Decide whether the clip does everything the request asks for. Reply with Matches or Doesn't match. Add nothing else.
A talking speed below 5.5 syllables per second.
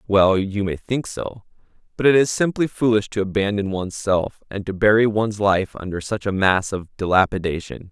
Matches